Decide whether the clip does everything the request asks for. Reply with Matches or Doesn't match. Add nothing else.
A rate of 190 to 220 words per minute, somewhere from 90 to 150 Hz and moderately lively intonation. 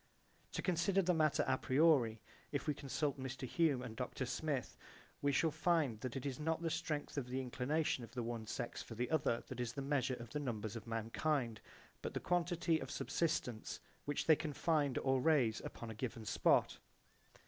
Matches